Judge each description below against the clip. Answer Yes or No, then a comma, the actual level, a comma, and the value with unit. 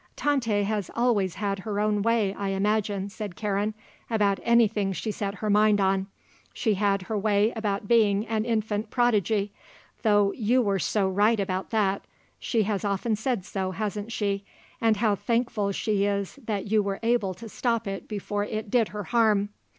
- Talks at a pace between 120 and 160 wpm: No, average, 175 wpm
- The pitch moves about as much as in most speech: No, narrow, 1.9 semitones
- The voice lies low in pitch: No, high, 210 Hz